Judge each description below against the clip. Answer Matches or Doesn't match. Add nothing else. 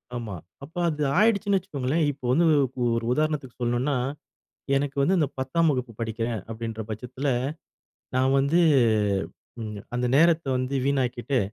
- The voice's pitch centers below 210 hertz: Matches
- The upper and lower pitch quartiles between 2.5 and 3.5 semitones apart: Doesn't match